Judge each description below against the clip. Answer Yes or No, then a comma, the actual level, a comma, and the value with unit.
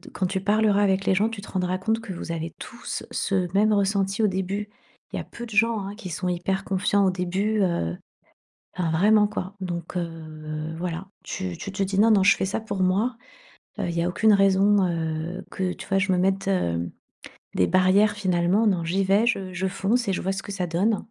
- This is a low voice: No, high, 190 Hz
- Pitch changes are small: Yes, narrow, 2.3 semitones